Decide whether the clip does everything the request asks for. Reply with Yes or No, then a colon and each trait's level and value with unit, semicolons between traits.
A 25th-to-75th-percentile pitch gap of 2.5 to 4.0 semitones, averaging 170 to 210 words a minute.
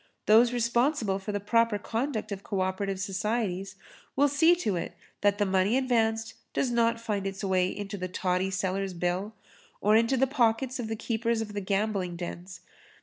Yes: average, 3.4 semitones; average, 175 wpm